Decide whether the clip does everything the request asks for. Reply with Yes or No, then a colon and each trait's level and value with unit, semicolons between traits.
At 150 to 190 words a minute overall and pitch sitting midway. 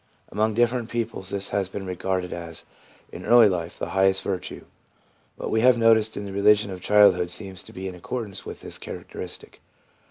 No: average, 185 wpm; low, 100 Hz